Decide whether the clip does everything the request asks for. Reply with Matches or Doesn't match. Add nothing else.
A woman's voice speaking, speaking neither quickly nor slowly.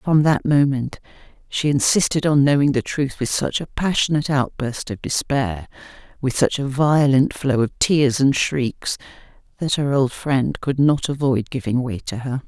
Matches